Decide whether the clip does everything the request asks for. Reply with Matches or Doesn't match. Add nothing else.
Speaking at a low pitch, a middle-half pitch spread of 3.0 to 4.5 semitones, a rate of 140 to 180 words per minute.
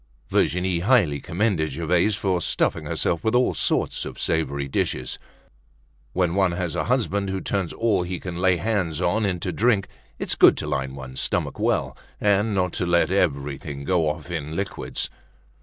Matches